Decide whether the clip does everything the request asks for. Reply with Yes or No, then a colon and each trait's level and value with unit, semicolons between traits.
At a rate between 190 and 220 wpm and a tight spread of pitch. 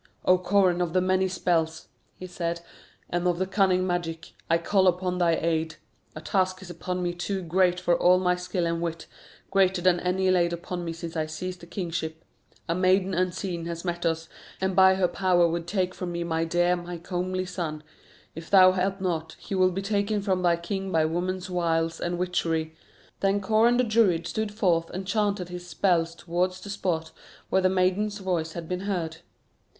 Yes: average, 195 wpm; narrow, 1.9 semitones